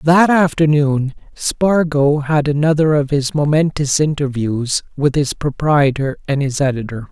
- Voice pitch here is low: No, medium, 145 Hz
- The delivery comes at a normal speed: No, slow, 125 wpm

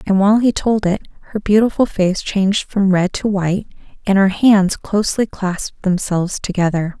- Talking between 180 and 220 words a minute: No, average, 170 wpm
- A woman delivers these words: Yes, female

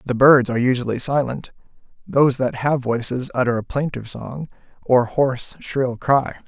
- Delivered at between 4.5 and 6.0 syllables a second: Yes, 5.0 syllables/s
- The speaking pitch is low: Yes, low, 130 Hz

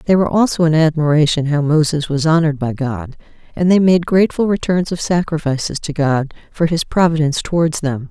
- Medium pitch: Yes, medium, 155 Hz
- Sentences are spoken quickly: No, average, 185 wpm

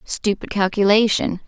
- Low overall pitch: No, high, 205 Hz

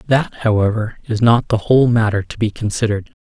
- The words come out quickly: No, average, 185 wpm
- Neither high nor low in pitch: No, low, 110 Hz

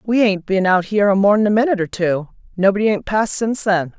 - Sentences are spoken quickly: Yes, fast, 225 wpm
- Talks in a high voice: Yes, high, 200 Hz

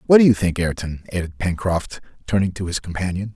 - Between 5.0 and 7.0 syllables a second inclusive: Yes, 5.9 syllables/s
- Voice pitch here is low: Yes, very low, 95 Hz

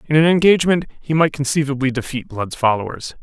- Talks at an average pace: Yes, average, 165 wpm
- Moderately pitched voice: Yes, medium, 145 Hz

